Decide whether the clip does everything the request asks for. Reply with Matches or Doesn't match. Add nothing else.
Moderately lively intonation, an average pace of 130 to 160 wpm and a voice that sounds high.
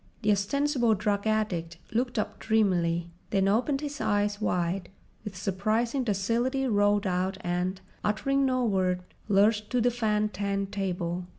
Matches